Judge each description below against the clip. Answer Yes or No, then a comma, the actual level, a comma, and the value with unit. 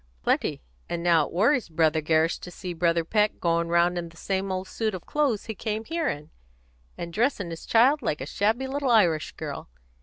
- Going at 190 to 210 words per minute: Yes, fast, 205 wpm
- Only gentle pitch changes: No, average, 5.1 semitones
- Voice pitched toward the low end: No, medium, 180 Hz